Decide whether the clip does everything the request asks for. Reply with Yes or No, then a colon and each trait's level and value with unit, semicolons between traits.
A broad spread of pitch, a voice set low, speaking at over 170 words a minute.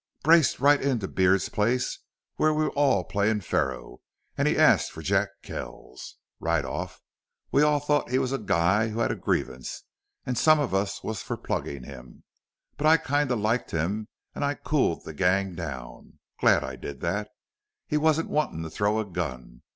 Yes: wide, 8.9 semitones; low, 105 Hz; average, 180 wpm